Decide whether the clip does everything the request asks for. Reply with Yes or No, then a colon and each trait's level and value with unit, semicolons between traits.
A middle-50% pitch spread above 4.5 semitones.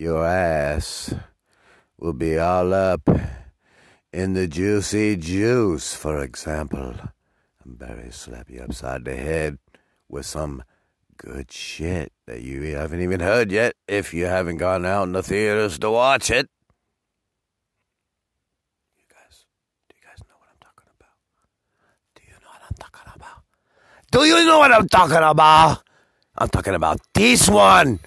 Yes: average, 5.3 semitones